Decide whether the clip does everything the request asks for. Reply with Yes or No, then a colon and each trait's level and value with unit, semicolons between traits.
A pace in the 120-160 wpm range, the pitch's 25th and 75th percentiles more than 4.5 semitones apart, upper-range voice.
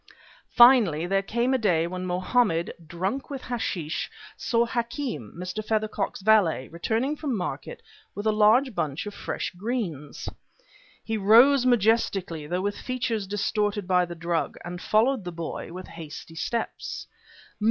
Yes: average, 140 wpm; average, 5.2 semitones; high, 205 Hz